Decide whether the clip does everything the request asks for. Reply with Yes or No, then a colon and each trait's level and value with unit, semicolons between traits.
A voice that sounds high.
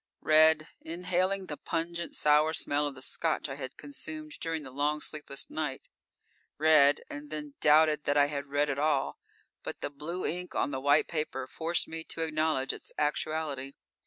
No: medium, 150 Hz